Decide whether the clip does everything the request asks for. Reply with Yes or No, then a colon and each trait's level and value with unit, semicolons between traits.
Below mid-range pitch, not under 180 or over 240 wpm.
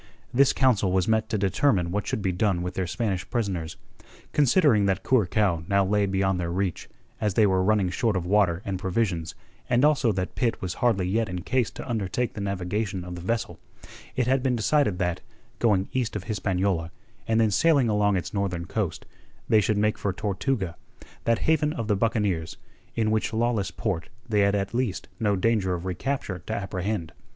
Yes: low, 100 Hz; average, 190 wpm